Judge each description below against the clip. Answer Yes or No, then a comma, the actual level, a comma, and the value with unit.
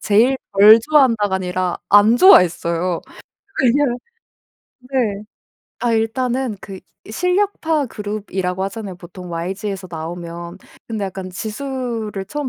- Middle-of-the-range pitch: No, high, 205 Hz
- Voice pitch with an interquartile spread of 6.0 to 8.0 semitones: No, average, 5.1 semitones